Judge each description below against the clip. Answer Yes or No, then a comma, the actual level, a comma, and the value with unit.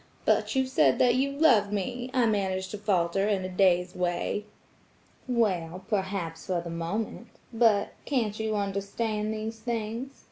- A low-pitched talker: No, high, 210 Hz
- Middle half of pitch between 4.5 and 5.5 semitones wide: No, average, 3.5 semitones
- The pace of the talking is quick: No, average, 145 wpm